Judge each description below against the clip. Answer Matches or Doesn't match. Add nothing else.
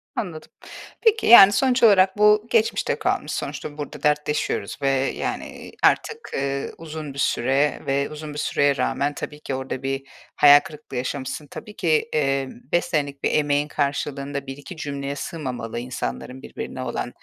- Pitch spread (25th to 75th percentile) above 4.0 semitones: Doesn't match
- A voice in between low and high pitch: Matches